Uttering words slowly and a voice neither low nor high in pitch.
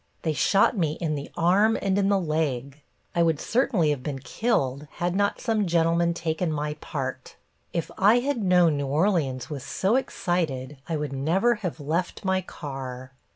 No: average, 175 wpm; medium, 165 Hz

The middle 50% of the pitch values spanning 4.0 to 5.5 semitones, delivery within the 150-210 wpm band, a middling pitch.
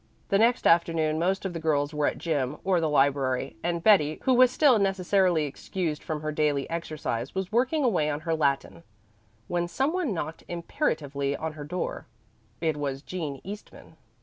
Yes: average, 4.4 semitones; average, 175 wpm; medium, 160 Hz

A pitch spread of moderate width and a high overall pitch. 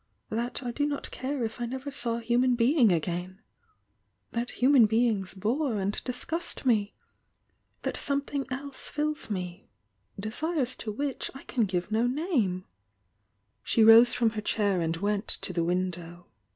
No: wide, 5.8 semitones; high, 225 Hz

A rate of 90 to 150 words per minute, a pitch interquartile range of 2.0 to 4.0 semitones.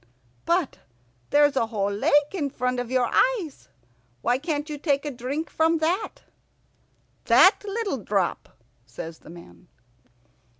No: slow, 135 wpm; wide, 5.4 semitones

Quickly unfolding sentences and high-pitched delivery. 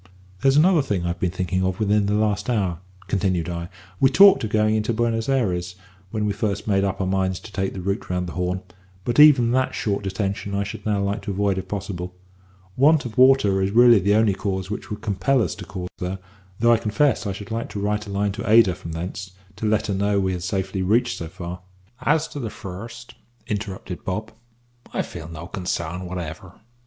No: fast, 220 wpm; low, 100 Hz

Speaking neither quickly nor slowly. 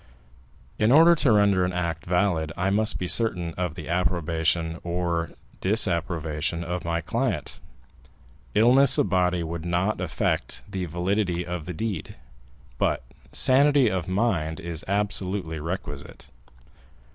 No: slow, 130 wpm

